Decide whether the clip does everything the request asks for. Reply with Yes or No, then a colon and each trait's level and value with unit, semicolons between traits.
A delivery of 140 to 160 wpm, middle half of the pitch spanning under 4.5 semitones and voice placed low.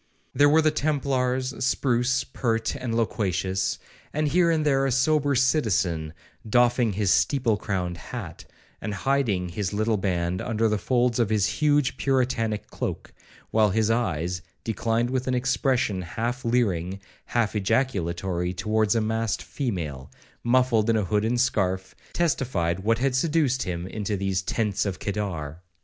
No: average, 150 wpm; average, 5.1 semitones; low, 115 Hz